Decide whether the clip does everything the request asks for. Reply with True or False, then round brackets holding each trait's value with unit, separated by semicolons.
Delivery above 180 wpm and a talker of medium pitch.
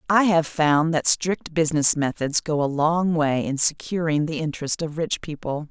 True (190 wpm; 155 Hz)